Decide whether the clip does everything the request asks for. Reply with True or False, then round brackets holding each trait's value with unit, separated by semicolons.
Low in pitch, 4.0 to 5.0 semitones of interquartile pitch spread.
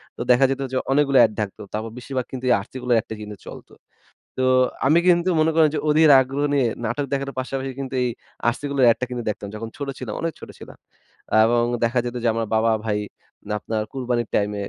False (125 Hz; 3.4 semitones)